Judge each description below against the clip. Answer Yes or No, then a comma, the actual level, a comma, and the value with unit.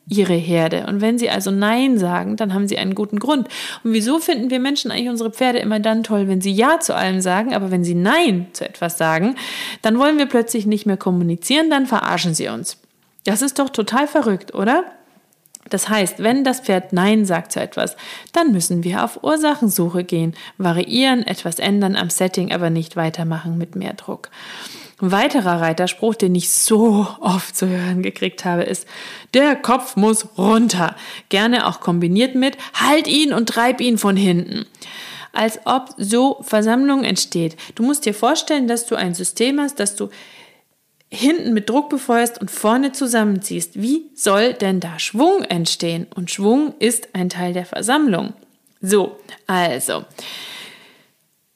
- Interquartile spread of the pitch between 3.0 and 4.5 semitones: No, wide, 5.5 semitones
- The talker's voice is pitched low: No, high, 215 Hz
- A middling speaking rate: Yes, average, 170 wpm